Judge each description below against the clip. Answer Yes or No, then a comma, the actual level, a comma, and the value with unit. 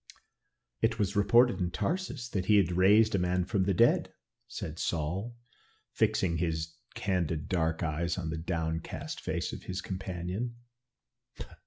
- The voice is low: Yes, very low, 90 Hz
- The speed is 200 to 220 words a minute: No, average, 145 wpm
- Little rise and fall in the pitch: No, average, 3.8 semitones